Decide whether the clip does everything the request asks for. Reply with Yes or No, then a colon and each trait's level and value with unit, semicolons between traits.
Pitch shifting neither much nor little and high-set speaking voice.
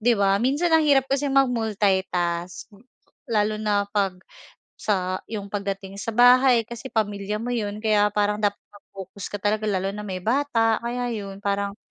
Yes: average, 3.0 semitones; high, 210 Hz